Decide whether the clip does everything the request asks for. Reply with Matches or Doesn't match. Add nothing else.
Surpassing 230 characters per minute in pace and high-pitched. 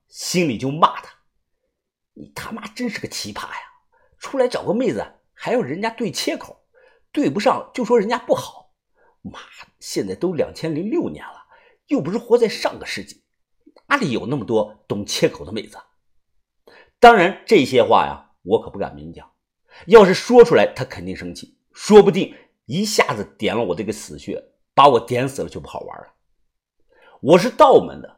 Matches